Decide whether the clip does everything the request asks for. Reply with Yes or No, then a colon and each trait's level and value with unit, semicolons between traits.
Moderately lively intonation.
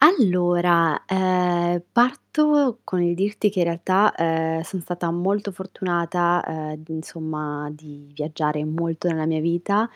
Yes: average, 3.0 semitones